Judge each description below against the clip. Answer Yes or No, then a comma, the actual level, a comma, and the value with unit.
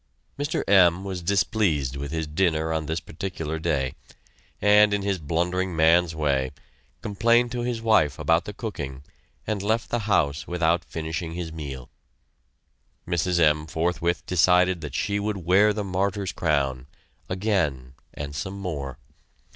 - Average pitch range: Yes, average, 4.4 semitones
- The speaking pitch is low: Yes, very low, 85 Hz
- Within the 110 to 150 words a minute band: Yes, average, 145 wpm